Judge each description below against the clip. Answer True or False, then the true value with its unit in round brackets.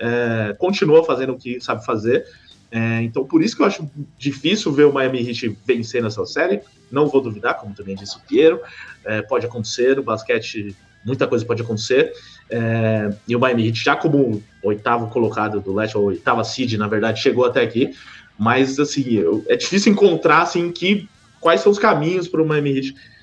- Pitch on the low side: True (120 Hz)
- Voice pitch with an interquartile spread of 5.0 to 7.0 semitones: True (5.3 semitones)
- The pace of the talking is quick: True (190 wpm)